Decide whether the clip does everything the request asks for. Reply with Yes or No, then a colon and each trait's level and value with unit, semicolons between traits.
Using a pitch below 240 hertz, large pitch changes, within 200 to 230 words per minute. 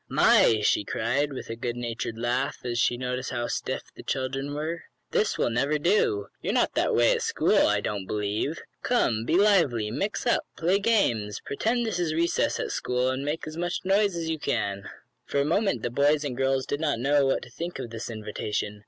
Yes: low, 135 Hz; wide, 6.3 semitones; fast, 205 wpm